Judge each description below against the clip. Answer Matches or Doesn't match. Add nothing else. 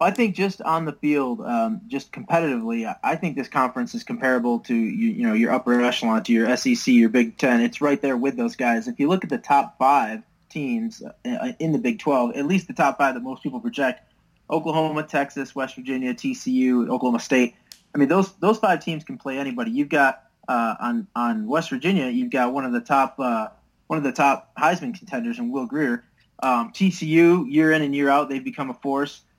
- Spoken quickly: Matches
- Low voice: Doesn't match